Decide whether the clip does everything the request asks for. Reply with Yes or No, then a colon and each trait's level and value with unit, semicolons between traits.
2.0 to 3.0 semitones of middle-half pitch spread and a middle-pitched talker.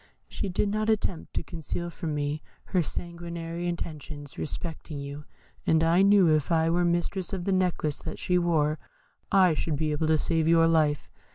Yes: narrow, 2.4 semitones; medium, 165 Hz